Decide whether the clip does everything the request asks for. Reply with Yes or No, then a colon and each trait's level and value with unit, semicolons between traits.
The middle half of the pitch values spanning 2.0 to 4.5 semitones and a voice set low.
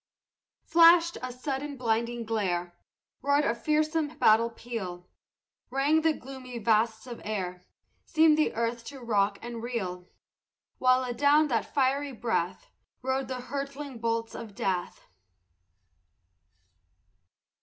No: average, 4.2 semitones; high, 245 Hz